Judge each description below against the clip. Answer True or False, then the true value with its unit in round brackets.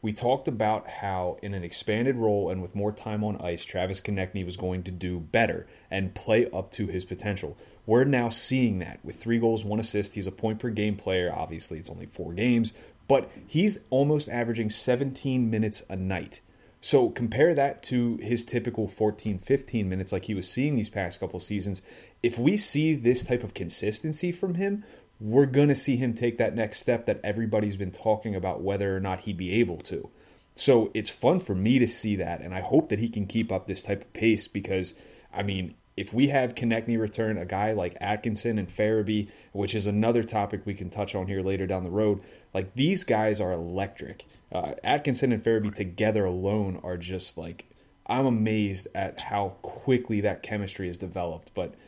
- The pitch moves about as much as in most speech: True (3.8 semitones)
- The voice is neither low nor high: False (105 Hz)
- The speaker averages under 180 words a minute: False (200 wpm)